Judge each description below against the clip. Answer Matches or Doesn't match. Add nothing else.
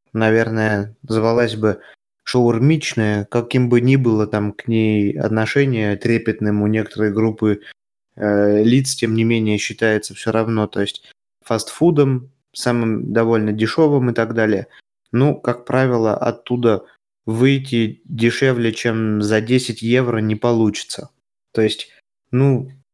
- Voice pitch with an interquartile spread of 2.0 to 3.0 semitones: Matches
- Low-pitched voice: Matches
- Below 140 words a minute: Matches